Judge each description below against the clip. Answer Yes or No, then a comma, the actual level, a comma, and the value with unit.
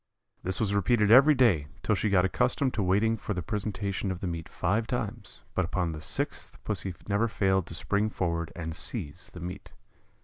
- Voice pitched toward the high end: No, low, 100 Hz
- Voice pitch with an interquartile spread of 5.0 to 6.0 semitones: No, average, 3.6 semitones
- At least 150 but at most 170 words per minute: No, average, 195 wpm